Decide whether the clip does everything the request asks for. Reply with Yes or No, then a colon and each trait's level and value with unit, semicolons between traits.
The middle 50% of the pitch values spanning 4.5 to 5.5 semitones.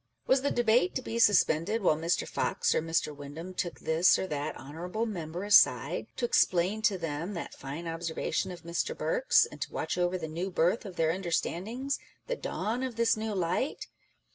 Yes: average, 5.2 semitones